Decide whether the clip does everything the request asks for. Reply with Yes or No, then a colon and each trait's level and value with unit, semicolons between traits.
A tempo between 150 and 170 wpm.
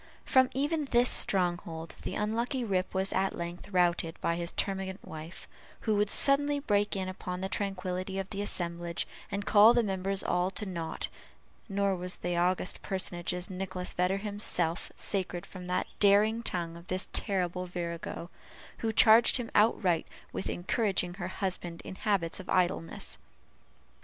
Yes: average, 155 wpm